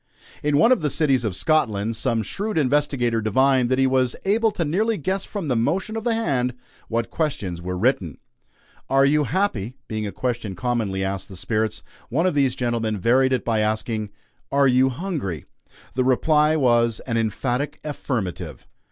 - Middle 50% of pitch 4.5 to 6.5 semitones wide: Yes, average, 5.2 semitones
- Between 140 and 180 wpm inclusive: Yes, average, 175 wpm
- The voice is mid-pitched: No, low, 130 Hz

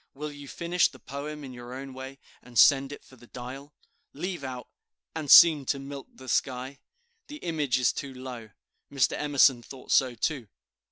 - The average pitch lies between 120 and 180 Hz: Yes, low, 135 Hz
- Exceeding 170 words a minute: Yes, average, 180 wpm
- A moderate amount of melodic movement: No, narrow, 2.2 semitones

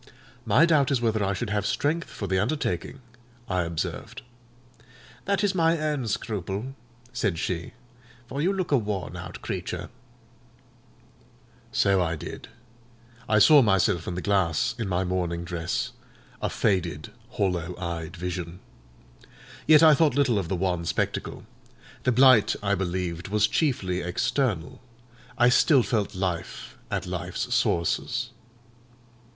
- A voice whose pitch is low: Yes, low, 100 Hz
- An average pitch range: No, wide, 6.4 semitones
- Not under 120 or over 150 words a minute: Yes, slow, 135 wpm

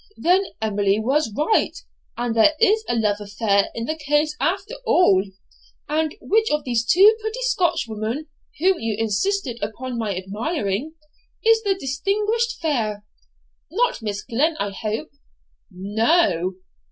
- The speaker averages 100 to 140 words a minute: Yes, slow, 135 wpm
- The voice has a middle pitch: No, very high, 270 Hz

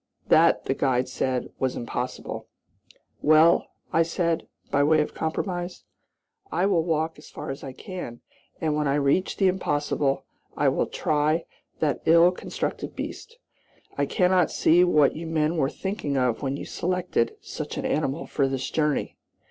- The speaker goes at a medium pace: Yes, average, 160 wpm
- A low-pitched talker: No, medium, 155 Hz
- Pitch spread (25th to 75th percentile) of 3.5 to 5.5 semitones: Yes, average, 3.8 semitones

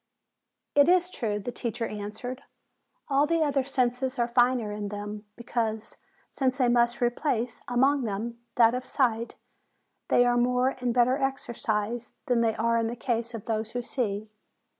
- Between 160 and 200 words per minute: Yes, average, 165 wpm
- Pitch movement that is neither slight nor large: No, narrow, 2.3 semitones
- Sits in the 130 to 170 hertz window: No, high, 240 Hz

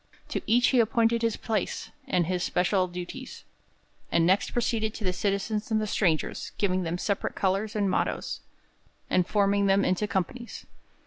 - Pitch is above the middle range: Yes, high, 200 Hz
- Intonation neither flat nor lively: Yes, average, 3.1 semitones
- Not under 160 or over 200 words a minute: Yes, average, 165 wpm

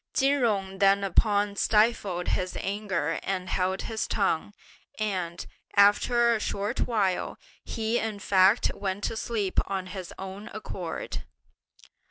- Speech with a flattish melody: Yes, narrow, 2.3 semitones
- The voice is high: Yes, high, 200 Hz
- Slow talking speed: Yes, slow, 125 wpm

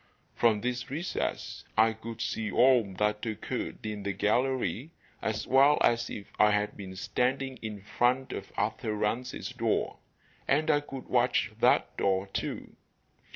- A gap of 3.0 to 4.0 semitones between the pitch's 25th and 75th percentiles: Yes, average, 3.4 semitones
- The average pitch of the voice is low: Yes, low, 115 Hz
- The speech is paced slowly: No, average, 150 wpm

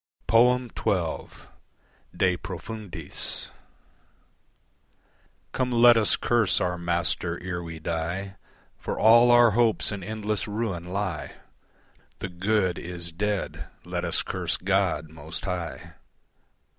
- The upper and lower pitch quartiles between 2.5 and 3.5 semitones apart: No, average, 4.2 semitones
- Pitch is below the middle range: Yes, very low, 95 Hz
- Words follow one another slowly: Yes, slow, 105 wpm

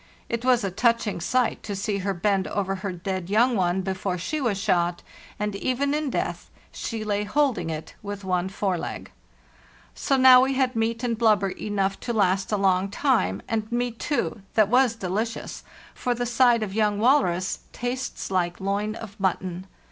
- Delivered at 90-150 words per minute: No, average, 180 wpm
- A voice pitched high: Yes, high, 210 Hz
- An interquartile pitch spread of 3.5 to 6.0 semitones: Yes, average, 4.0 semitones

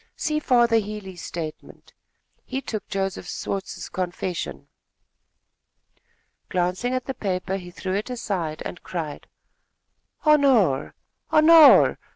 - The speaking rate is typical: No, slow, 105 wpm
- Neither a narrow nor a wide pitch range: No, wide, 6.0 semitones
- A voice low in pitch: No, high, 195 Hz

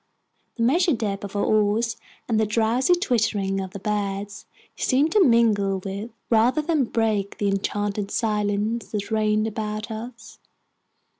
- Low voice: No, high, 215 Hz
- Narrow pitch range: Yes, narrow, 2.3 semitones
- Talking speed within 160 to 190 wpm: No, average, 145 wpm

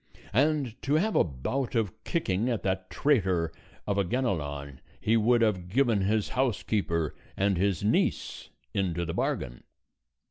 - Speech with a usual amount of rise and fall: No, wide, 5.8 semitones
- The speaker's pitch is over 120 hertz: No, low, 100 Hz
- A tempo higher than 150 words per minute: No, average, 145 wpm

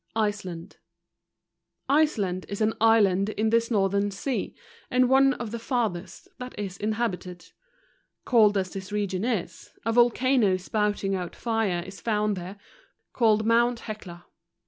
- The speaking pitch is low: No, high, 210 Hz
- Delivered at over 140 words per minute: No, slow, 135 wpm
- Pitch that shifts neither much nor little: Yes, average, 3.5 semitones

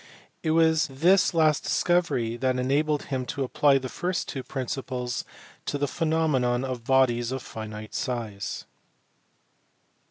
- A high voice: No, low, 135 Hz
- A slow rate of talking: Yes, slow, 130 wpm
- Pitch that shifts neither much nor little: Yes, average, 4.1 semitones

